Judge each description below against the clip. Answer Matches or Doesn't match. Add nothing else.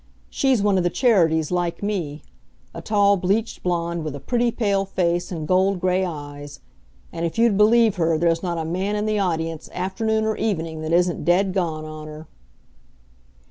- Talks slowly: Doesn't match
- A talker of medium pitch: Matches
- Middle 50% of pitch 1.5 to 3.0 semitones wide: Doesn't match